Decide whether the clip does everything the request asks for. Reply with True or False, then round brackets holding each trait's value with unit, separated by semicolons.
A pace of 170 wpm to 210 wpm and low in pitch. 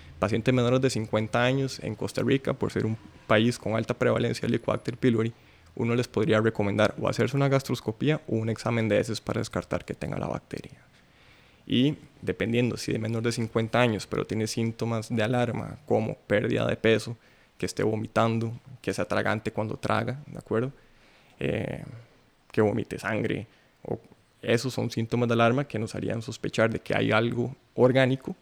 True (175 wpm; 115 Hz)